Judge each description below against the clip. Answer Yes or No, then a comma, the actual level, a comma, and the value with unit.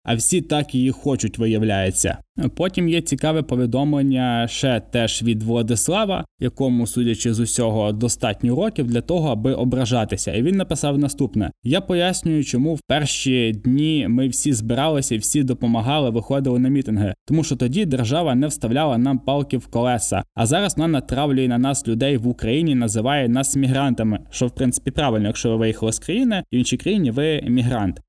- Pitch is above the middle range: No, low, 125 Hz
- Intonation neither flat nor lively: Yes, average, 3.6 semitones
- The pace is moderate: No, fast, 165 wpm